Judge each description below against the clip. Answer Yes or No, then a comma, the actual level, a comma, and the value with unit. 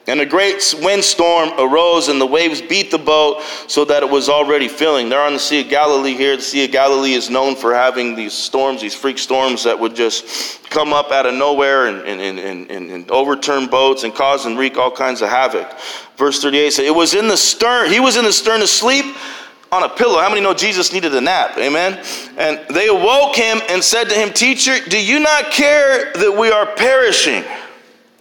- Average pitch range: No, wide, 7.6 semitones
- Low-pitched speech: No, medium, 150 Hz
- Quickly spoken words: Yes, fast, 215 wpm